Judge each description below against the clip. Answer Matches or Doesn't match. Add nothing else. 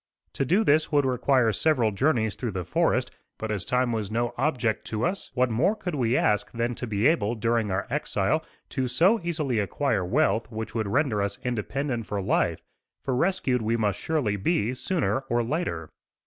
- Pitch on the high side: Doesn't match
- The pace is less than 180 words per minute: Doesn't match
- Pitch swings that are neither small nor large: Matches